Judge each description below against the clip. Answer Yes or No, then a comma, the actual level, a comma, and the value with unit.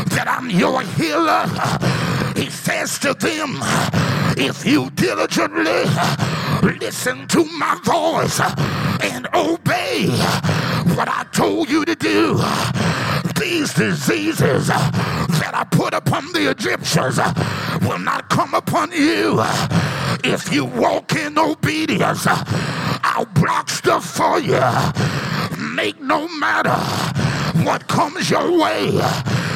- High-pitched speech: Yes, very high, 320 Hz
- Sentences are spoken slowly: Yes, slow, 110 wpm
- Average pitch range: No, narrow, 1.4 semitones